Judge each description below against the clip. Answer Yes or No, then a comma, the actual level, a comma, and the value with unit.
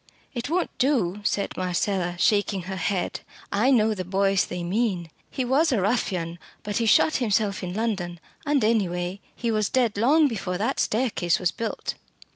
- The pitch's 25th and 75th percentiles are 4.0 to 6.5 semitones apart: Yes, average, 4.3 semitones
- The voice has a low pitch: No, high, 205 Hz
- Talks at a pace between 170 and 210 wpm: Yes, average, 175 wpm